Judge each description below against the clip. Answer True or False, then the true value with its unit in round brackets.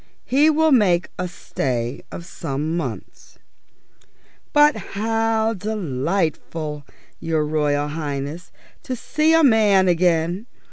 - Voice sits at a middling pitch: True (175 Hz)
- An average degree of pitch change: False (6.9 semitones)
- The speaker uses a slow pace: True (105 wpm)